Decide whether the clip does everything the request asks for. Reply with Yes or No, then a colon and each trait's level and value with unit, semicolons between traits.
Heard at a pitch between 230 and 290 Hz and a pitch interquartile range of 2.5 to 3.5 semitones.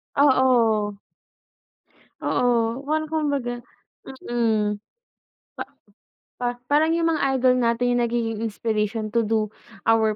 Yes: high, 240 Hz; average, 2.9 semitones